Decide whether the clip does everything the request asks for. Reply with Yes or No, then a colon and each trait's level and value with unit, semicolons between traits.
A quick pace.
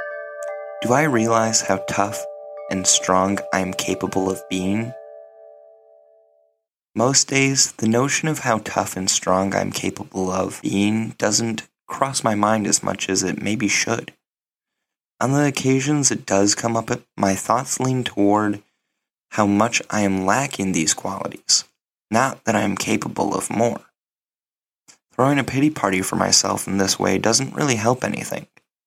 No: average, 155 wpm